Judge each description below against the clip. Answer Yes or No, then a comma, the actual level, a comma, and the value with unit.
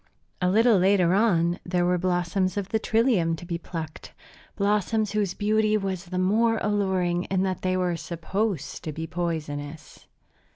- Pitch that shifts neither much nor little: Yes, average, 3.2 semitones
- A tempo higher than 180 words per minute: No, average, 165 wpm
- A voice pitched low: No, medium, 185 Hz